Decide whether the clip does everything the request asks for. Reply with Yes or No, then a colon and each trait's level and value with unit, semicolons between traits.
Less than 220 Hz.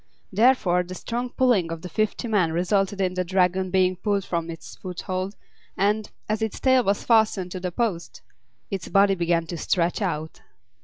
Yes: high, 190 Hz